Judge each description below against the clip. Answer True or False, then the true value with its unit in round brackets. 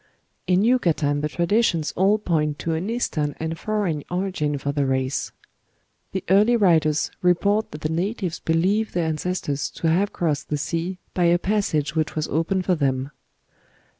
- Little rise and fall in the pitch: False (4.1 semitones)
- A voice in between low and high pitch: True (170 Hz)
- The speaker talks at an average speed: True (165 wpm)